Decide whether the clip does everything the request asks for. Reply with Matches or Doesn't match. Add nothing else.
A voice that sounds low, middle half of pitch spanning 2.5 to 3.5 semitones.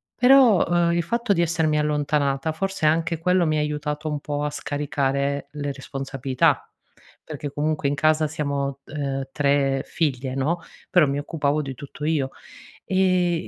Doesn't match